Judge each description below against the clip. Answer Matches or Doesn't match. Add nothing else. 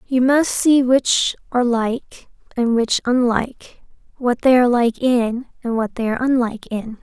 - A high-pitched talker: Matches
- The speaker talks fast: Doesn't match